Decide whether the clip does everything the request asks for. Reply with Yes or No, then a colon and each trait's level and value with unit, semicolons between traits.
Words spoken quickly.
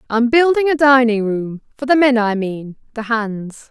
No: average, 160 wpm